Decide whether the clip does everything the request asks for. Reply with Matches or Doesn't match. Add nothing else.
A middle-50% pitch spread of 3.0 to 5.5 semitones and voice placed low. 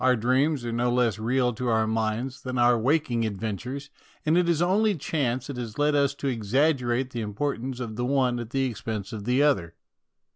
Matches